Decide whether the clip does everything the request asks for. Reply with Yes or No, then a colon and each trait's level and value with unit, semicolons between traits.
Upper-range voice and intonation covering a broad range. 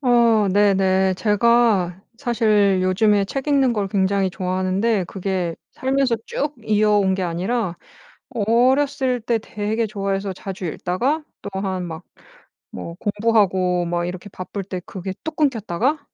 No: high, 205 Hz; average, 3.8 semitones